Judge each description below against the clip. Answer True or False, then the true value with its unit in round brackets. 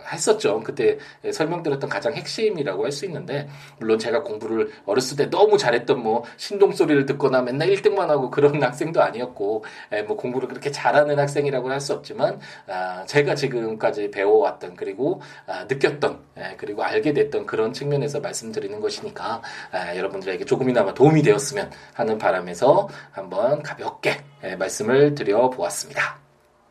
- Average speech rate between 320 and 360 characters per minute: True (355 characters per minute)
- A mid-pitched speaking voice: True (145 Hz)